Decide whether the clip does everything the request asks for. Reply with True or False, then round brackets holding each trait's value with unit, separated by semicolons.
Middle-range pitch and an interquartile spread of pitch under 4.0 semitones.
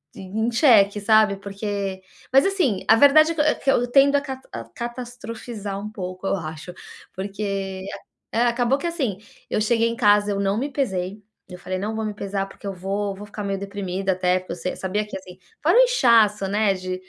False (205 Hz; 3.5 semitones)